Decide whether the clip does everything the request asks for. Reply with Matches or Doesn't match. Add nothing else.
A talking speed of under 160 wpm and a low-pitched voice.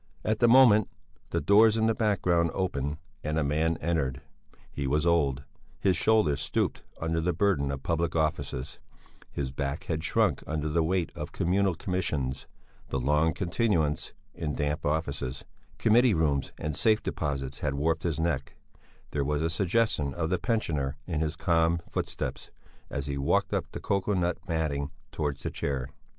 Doesn't match